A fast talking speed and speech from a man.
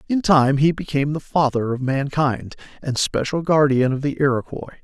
No: average, 175 wpm; male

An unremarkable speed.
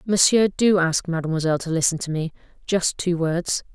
Yes: average, 160 wpm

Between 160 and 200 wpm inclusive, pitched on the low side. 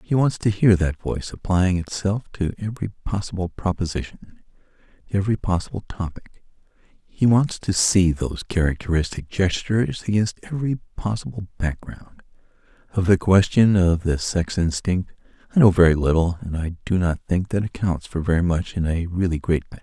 Yes: average, 165 wpm; very low, 95 Hz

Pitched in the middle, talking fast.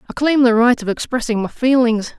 No: high, 240 Hz; fast, 220 wpm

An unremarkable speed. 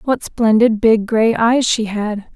Yes: average, 180 wpm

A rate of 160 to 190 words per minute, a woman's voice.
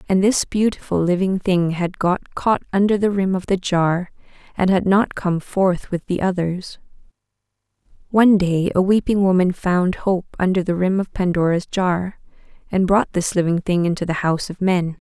Yes: average, 180 wpm; female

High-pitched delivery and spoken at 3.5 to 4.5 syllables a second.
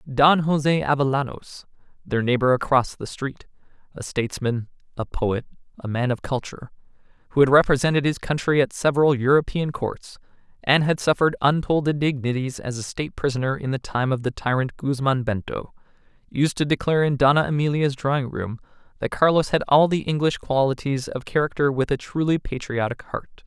No: medium, 140 Hz; 4.3 syllables/s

